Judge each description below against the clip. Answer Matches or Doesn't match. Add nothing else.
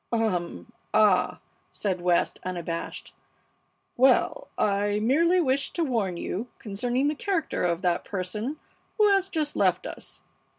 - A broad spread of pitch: Matches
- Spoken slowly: Matches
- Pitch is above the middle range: Matches